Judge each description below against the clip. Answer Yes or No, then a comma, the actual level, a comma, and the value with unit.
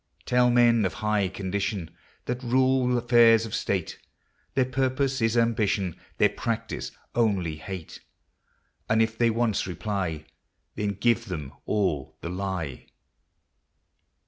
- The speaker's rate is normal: No, slow, 120 wpm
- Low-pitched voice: Yes, low, 110 Hz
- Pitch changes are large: No, average, 4.2 semitones